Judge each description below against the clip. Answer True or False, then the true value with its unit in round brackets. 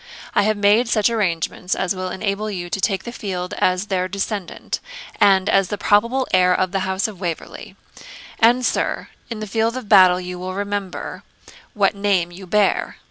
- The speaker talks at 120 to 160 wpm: False (185 wpm)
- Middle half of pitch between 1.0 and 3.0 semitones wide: True (2.4 semitones)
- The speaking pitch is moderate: False (195 Hz)